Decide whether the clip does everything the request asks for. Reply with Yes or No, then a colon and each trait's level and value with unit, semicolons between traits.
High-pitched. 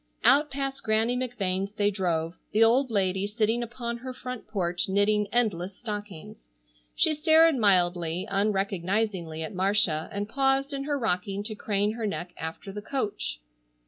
Yes: high, 210 Hz